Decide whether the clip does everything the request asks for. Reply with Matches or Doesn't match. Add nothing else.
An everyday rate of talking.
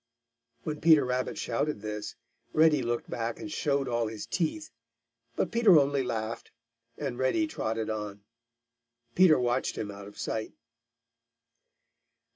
Doesn't match